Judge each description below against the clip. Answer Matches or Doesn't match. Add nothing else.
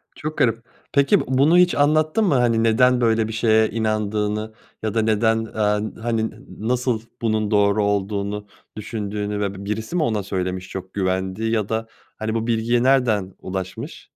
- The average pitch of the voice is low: Matches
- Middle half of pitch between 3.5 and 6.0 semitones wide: Doesn't match